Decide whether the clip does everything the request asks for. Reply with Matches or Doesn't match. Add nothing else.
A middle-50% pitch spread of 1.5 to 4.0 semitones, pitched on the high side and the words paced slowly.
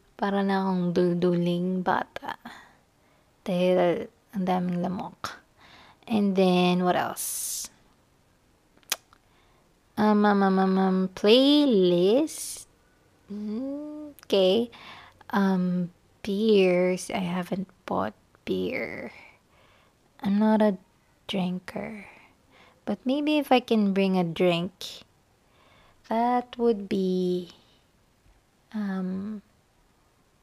Matches